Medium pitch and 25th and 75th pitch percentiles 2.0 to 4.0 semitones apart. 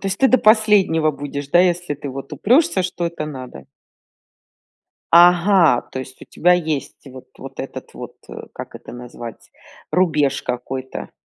No: medium, 155 Hz; average, 5.3 semitones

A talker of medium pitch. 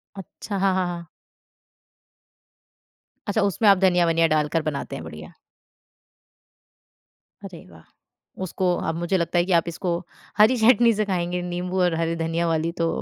Yes: medium, 175 Hz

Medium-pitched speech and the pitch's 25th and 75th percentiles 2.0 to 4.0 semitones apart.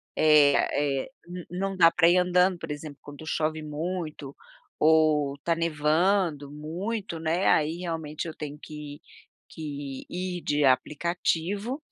Yes: medium, 160 Hz; average, 3.1 semitones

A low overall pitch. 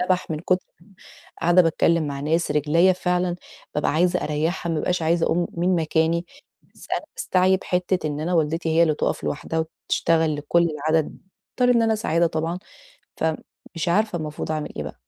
No: medium, 165 Hz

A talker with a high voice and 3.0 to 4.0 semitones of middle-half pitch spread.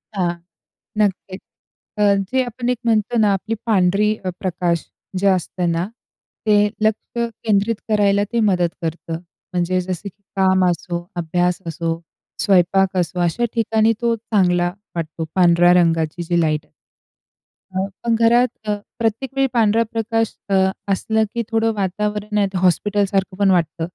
Yes: high, 195 Hz; average, 3.7 semitones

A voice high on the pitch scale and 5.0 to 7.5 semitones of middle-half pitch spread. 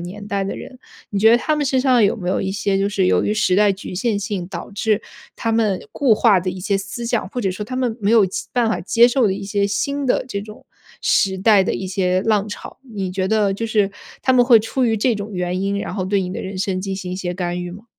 No: high, 200 Hz; average, 3.0 semitones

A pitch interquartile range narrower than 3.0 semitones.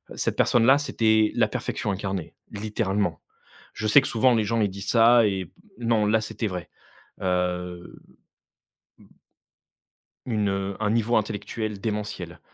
Yes: narrow, 2.6 semitones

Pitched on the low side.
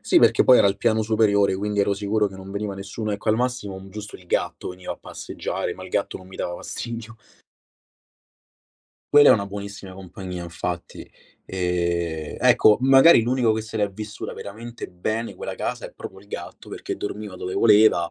Yes: low, 100 Hz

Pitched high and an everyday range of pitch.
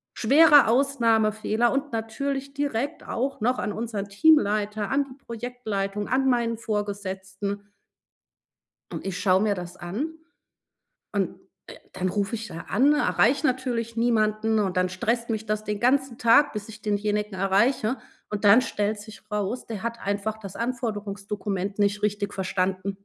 Yes: high, 215 Hz; average, 3.2 semitones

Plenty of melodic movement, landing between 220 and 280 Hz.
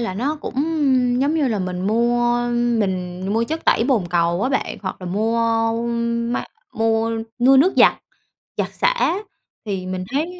Yes: wide, 5.9 semitones; high, 230 Hz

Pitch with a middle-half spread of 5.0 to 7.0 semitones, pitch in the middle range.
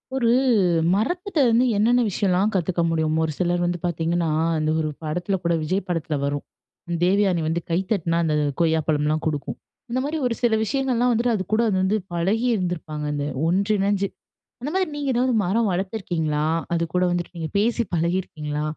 Yes: wide, 5.4 semitones; medium, 180 Hz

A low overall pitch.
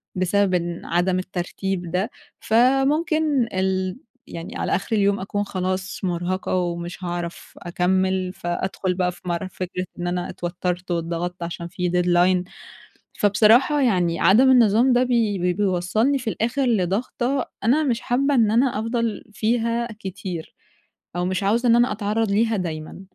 No: high, 190 Hz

